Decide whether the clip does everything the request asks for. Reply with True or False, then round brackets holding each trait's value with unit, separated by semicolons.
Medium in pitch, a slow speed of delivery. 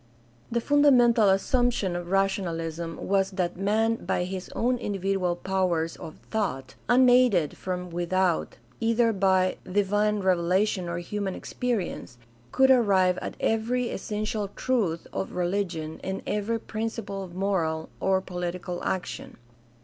False (195 Hz; 125 wpm)